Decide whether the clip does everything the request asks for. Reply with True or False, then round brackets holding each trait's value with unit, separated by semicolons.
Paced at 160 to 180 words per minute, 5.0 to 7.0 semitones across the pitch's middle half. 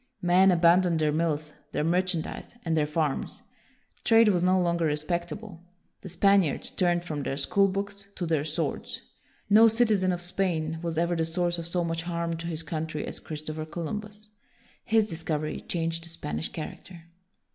False (170 wpm; 2.8 semitones)